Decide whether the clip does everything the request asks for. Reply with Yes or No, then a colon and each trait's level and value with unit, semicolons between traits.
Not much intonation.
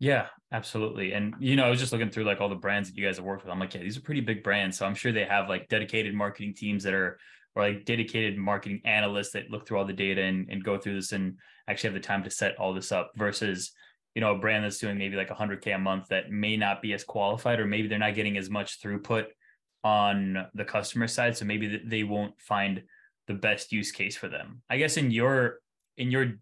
Yes: narrow, 1.9 semitones